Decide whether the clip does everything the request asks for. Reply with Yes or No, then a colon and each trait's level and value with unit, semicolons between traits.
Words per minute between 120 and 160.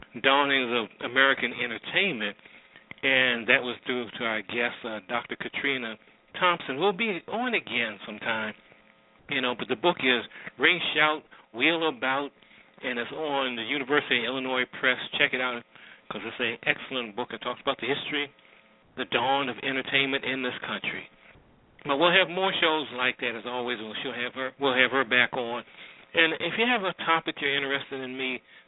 No: average, 180 wpm